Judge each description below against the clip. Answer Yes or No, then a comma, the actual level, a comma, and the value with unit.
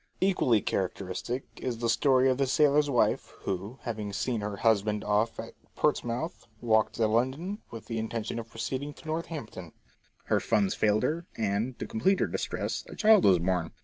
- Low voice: Yes, low, 115 Hz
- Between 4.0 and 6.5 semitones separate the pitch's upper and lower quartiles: Yes, average, 4.8 semitones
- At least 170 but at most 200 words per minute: Yes, average, 175 wpm